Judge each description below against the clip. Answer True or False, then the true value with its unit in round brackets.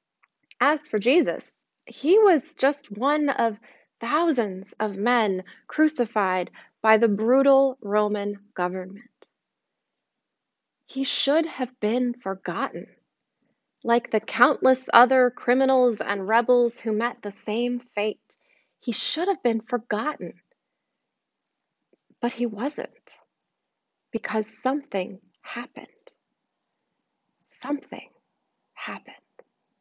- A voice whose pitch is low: False (240 Hz)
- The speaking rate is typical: False (95 wpm)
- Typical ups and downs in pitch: True (4.0 semitones)